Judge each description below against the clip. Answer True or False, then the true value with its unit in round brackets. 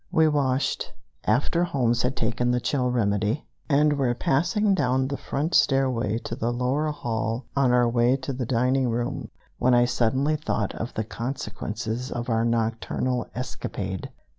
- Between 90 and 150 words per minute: False (160 wpm)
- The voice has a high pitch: False (125 Hz)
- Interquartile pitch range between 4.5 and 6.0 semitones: False (2.8 semitones)